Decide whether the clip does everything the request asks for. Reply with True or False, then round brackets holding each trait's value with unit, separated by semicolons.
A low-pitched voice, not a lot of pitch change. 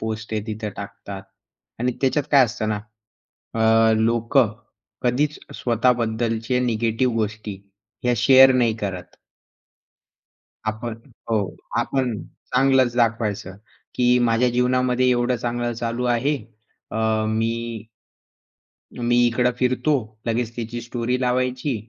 True (120 Hz; 2.1 semitones)